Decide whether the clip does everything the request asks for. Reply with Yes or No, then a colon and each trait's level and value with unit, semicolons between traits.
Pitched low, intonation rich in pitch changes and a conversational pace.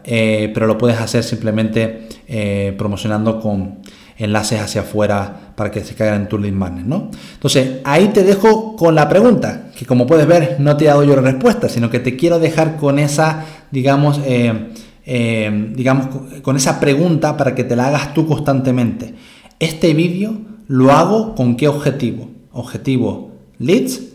Yes: low, 130 Hz; wide, 5.8 semitones; average, 170 wpm